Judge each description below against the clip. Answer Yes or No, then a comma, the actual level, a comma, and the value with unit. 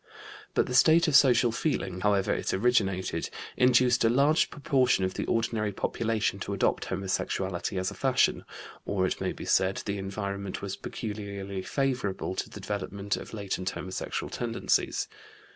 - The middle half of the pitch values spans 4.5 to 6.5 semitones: No, average, 4.0 semitones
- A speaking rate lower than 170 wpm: Yes, average, 155 wpm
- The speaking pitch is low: Yes, low, 100 Hz